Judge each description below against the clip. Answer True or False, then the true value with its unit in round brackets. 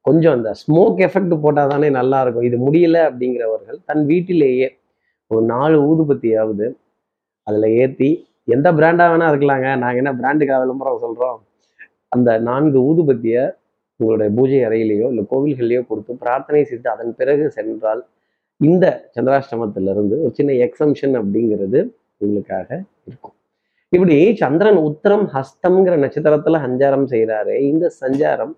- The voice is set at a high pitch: False (135 Hz)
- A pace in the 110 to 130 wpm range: True (120 wpm)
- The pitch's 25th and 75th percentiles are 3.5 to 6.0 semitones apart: True (4.9 semitones)